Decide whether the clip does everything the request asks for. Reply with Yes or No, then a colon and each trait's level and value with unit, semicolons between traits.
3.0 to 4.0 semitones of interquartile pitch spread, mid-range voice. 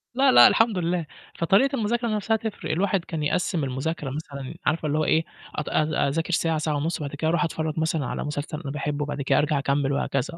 Yes: average, 3.5 semitones; medium, 160 Hz